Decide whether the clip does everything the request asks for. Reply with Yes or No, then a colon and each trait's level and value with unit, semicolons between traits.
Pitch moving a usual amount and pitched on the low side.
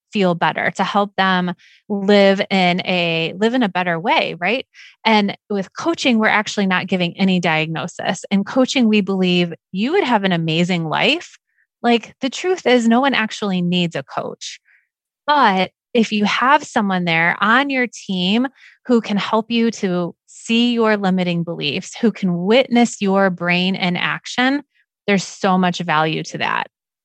No: average, 4.4 semitones; high, 200 Hz